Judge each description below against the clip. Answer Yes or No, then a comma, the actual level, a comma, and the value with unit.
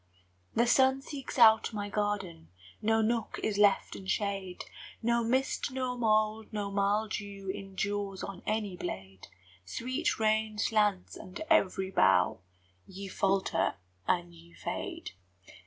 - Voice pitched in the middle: No, high, 205 Hz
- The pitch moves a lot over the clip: No, narrow, 2.5 semitones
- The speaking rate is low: Yes, slow, 125 wpm